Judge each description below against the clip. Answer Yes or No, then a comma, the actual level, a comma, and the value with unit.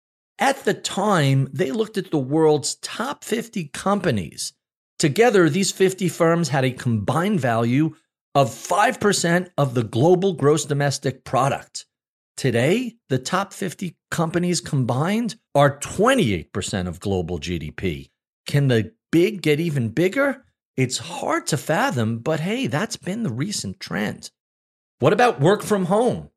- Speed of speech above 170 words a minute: No, slow, 135 wpm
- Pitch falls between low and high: Yes, medium, 155 Hz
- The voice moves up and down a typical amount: No, wide, 7.0 semitones